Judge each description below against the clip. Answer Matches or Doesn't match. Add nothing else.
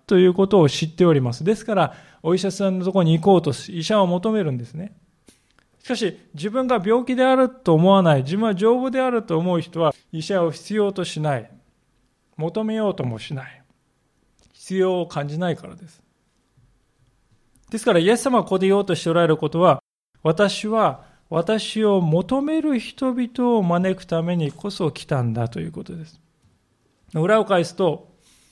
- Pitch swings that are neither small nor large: Matches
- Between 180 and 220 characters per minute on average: Doesn't match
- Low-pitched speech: Doesn't match